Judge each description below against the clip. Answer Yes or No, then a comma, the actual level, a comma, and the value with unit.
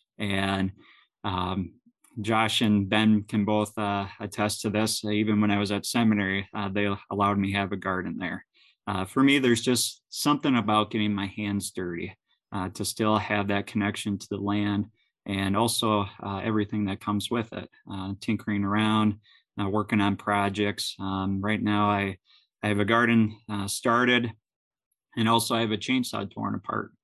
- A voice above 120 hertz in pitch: No, low, 105 Hz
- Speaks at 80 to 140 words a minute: No, average, 175 wpm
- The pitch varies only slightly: Yes, narrow, 1.5 semitones